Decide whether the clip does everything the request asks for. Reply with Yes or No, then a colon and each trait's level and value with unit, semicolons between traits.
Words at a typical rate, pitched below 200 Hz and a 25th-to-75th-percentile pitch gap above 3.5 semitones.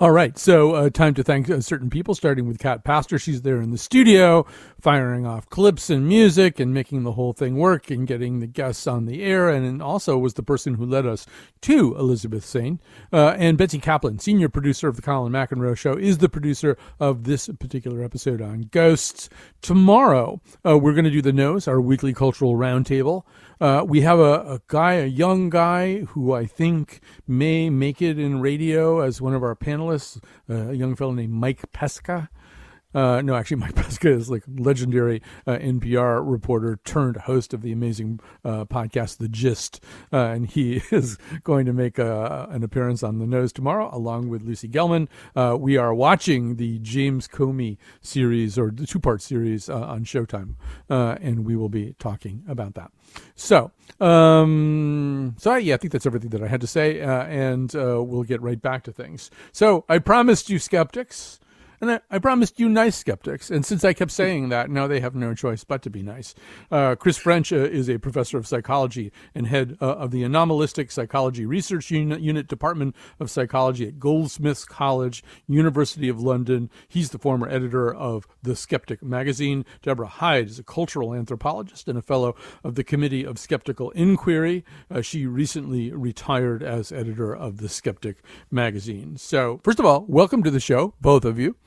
Yes: average, 190 wpm; low, 135 Hz; average, 4.1 semitones